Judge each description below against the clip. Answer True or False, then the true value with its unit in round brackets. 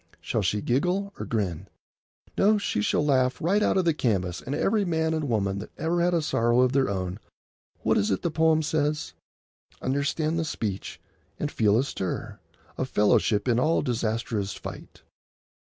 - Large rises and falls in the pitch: True (7.4 semitones)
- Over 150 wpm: True (175 wpm)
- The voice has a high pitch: False (130 Hz)